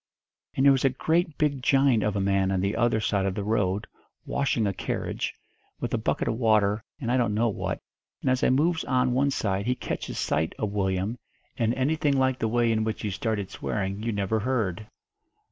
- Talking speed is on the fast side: Yes, fast, 215 wpm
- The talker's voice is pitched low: Yes, low, 110 Hz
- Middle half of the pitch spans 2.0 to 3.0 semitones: No, average, 4.5 semitones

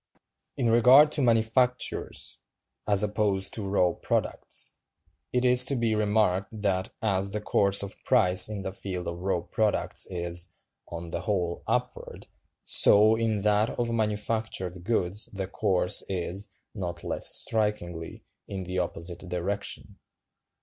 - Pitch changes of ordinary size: Yes, average, 3.3 semitones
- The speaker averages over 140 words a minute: No, slow, 135 wpm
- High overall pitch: No, low, 100 Hz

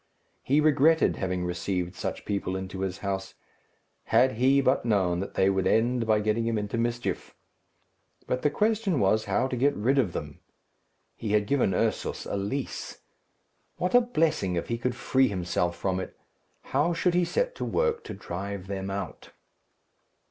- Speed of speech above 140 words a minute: Yes, average, 170 wpm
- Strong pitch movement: Yes, wide, 6.3 semitones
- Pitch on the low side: Yes, low, 110 Hz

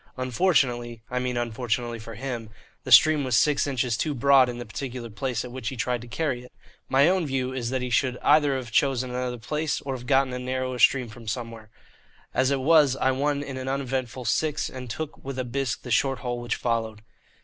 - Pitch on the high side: No, low, 130 Hz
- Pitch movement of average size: No, narrow, 2.2 semitones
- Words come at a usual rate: No, fast, 220 wpm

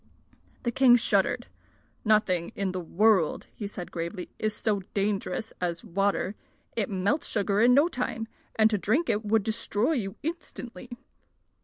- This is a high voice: Yes, high, 210 Hz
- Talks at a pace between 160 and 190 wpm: No, average, 150 wpm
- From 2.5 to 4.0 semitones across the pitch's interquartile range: Yes, average, 3.3 semitones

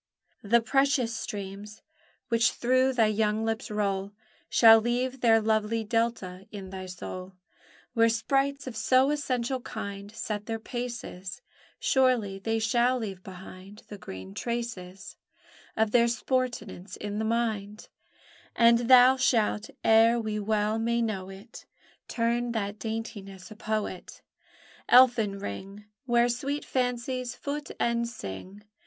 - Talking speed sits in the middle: No, slow, 130 wpm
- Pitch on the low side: No, high, 225 Hz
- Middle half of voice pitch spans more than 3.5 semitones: No, average, 2.9 semitones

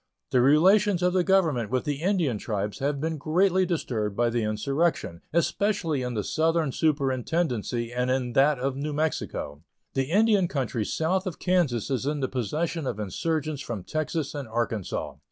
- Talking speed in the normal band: Yes, average, 170 wpm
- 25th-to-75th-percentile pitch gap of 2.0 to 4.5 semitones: No, wide, 5.5 semitones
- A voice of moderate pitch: Yes, medium, 145 Hz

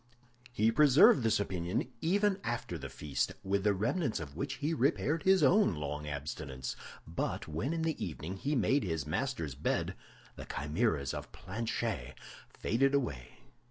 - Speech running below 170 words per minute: Yes, average, 155 wpm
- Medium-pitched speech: No, low, 105 Hz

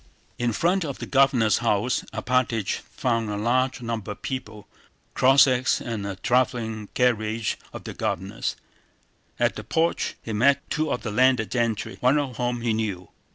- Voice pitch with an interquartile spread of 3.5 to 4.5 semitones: No, average, 2.9 semitones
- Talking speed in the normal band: Yes, average, 160 wpm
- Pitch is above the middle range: No, low, 120 Hz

